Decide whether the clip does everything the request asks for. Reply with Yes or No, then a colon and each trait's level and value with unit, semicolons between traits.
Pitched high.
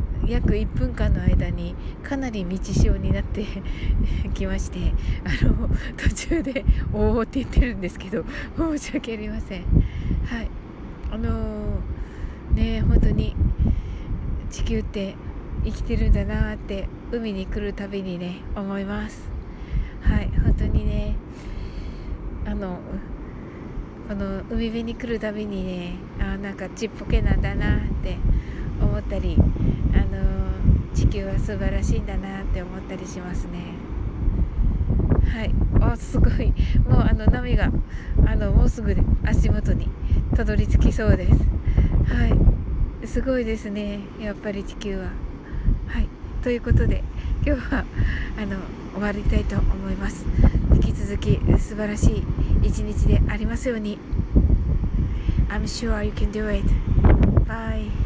No: low, 110 Hz